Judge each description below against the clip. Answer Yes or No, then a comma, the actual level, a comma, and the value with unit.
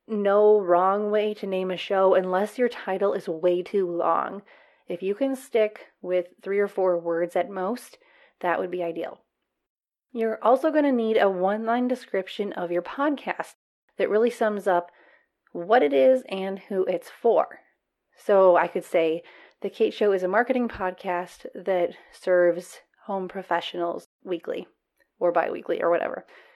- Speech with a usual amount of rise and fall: Yes, average, 3.8 semitones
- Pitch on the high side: Yes, high, 195 Hz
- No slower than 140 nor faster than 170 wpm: Yes, average, 165 wpm